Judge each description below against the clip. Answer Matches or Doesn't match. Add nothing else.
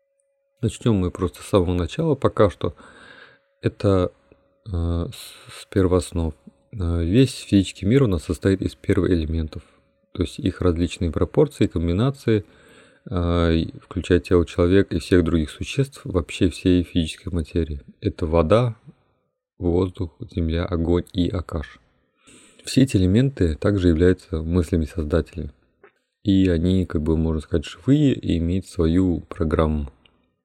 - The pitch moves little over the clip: Doesn't match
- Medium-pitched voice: Doesn't match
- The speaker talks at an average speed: Matches